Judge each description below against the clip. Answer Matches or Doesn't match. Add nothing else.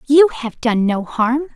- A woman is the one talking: Matches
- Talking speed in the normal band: Matches